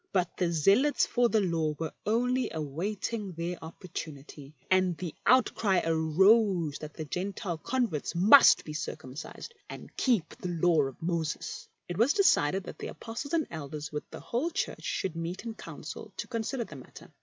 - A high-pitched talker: No, medium, 180 Hz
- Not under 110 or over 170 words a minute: Yes, average, 165 wpm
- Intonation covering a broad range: Yes, wide, 6.1 semitones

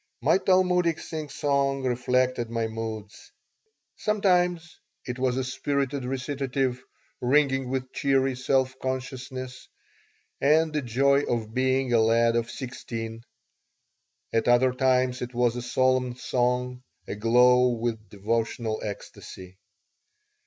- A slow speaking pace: Yes, slow, 110 wpm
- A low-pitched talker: Yes, low, 125 Hz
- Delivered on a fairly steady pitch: Yes, narrow, 2.3 semitones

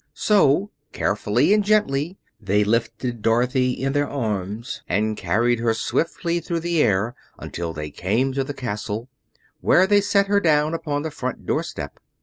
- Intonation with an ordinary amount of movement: No, wide, 7.1 semitones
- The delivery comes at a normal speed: Yes, average, 155 wpm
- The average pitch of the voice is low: Yes, low, 130 Hz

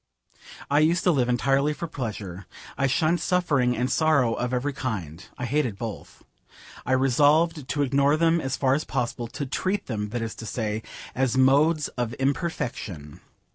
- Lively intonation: No, average, 4.2 semitones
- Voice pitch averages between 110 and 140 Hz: Yes, low, 135 Hz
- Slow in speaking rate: No, average, 170 wpm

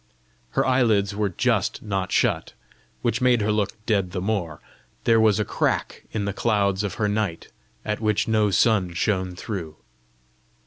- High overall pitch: No, low, 105 Hz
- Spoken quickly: No, average, 165 wpm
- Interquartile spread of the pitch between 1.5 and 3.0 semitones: Yes, narrow, 2.4 semitones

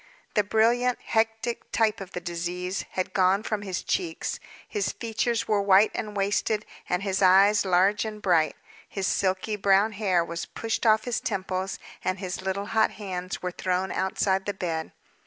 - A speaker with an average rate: Yes, average, 170 wpm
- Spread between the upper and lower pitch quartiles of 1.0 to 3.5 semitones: Yes, average, 2.8 semitones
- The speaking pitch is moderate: No, high, 195 Hz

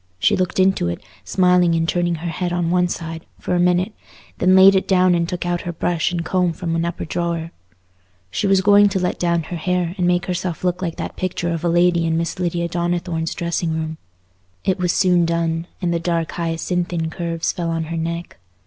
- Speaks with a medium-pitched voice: Yes, medium, 175 Hz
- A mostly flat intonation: Yes, narrow, 1.3 semitones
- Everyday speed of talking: No, fast, 215 wpm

